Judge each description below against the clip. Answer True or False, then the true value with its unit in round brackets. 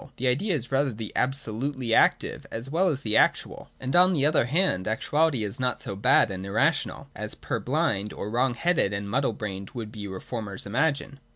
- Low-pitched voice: True (125 Hz)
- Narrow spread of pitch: False (4.9 semitones)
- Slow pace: False (185 wpm)